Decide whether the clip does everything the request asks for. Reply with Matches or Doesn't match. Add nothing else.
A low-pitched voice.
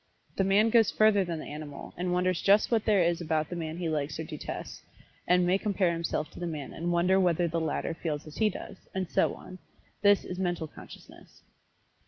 Doesn't match